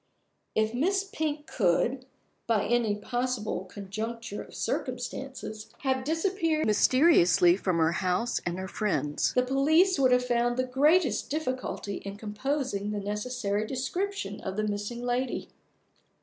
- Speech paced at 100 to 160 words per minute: Yes, slow, 135 wpm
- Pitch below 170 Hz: No, high, 240 Hz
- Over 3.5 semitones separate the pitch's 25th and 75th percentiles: Yes, average, 4.7 semitones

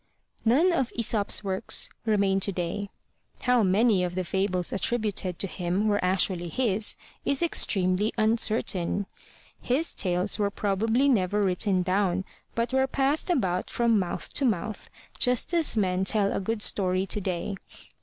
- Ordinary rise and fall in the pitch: Yes, average, 3.8 semitones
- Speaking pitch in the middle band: No, high, 200 Hz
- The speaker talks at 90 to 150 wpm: Yes, average, 145 wpm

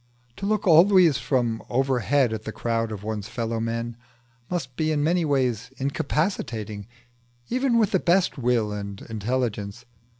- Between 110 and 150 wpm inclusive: Yes, average, 145 wpm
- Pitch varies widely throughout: Yes, wide, 5.9 semitones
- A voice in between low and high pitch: No, low, 125 Hz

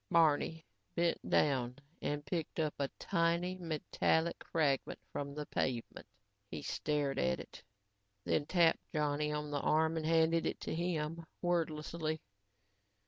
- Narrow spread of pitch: Yes, narrow, 2.2 semitones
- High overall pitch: No, medium, 155 Hz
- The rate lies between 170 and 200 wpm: No, slow, 135 wpm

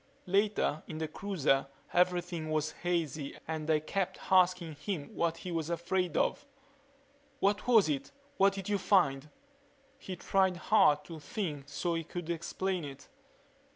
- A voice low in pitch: No, medium, 170 Hz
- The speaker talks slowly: No, average, 150 wpm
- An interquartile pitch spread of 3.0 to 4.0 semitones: Yes, average, 3.6 semitones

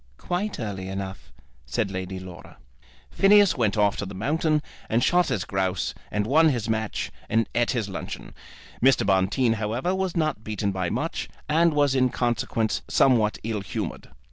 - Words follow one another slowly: No, average, 165 wpm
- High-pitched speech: No, low, 115 Hz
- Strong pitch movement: Yes, wide, 6.7 semitones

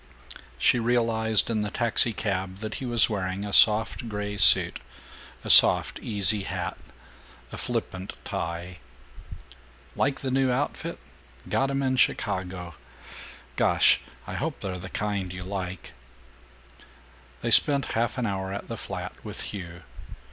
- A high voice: No, low, 105 Hz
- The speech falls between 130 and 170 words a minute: Yes, slow, 135 wpm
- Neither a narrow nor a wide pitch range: Yes, average, 4.0 semitones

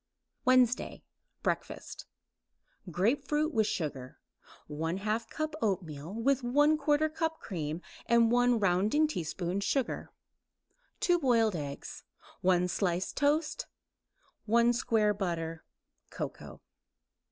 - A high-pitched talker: Yes, high, 225 Hz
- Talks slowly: Yes, slow, 95 wpm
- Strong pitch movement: Yes, wide, 7.6 semitones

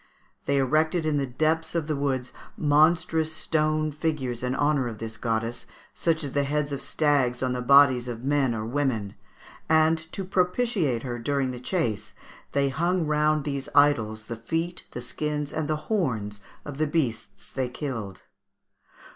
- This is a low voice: No, medium, 145 Hz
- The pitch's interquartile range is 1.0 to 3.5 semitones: No, average, 4.0 semitones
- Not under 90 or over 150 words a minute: No, average, 165 wpm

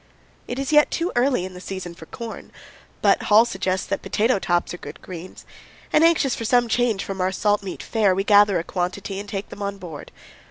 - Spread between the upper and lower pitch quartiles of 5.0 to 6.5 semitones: No, average, 4.0 semitones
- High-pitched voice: Yes, high, 200 Hz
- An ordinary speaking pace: No, fast, 210 wpm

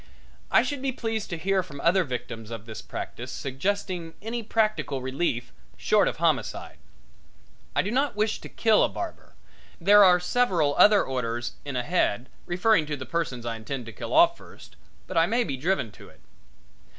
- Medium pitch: Yes, medium, 170 Hz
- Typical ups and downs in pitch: No, wide, 8.5 semitones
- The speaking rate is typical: Yes, average, 180 wpm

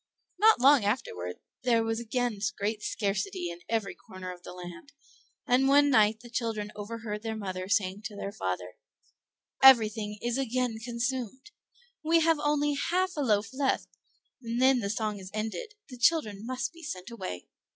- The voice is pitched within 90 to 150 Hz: No, high, 225 Hz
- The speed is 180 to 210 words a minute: No, average, 165 wpm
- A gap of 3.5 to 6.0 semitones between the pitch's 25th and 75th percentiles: Yes, average, 4.5 semitones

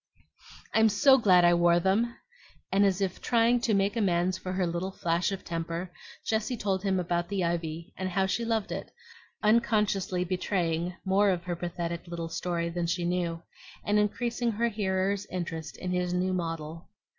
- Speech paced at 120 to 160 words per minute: No, average, 175 wpm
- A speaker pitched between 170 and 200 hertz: Yes, medium, 185 Hz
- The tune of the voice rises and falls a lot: No, average, 3.0 semitones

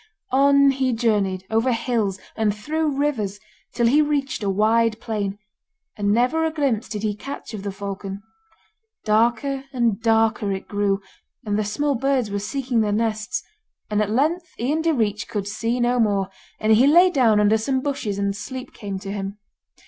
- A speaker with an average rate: Yes, average, 175 wpm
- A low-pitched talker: No, high, 225 Hz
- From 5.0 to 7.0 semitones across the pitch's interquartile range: No, average, 4.5 semitones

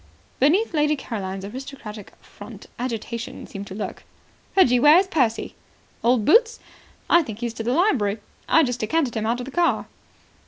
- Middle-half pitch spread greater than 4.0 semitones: Yes, wide, 5.6 semitones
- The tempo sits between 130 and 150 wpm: No, average, 170 wpm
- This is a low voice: No, high, 245 Hz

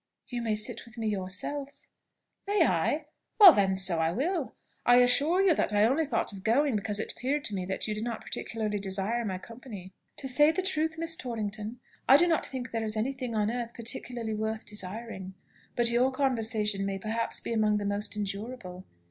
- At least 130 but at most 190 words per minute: No, average, 200 wpm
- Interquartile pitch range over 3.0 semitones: Yes, average, 4.0 semitones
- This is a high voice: Yes, high, 225 Hz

